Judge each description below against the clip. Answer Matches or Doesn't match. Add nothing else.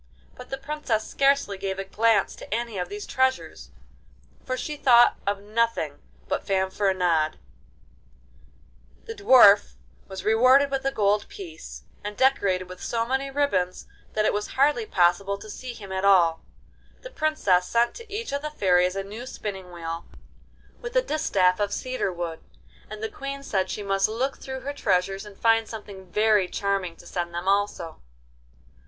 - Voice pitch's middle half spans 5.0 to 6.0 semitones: Matches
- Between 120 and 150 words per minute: Doesn't match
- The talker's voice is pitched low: Doesn't match